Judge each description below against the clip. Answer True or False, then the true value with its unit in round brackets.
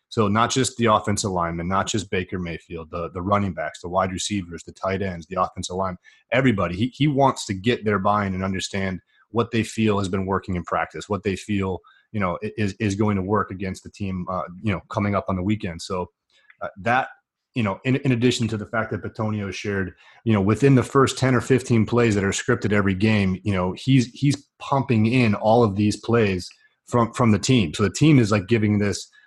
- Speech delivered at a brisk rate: True (230 wpm)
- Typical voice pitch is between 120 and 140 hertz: False (105 Hz)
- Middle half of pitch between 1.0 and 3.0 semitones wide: False (3.6 semitones)